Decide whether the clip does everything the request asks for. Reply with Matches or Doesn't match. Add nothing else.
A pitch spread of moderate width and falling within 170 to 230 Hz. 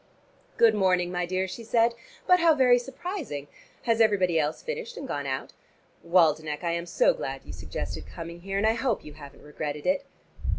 Doesn't match